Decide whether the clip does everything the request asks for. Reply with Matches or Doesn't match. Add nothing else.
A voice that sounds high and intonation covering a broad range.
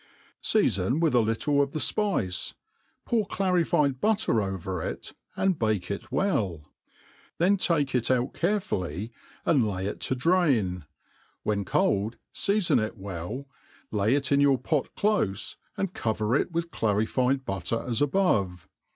Doesn't match